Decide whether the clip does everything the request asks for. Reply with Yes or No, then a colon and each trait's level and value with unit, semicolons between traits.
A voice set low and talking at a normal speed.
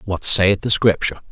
Yes: very low, 95 Hz; average, 185 wpm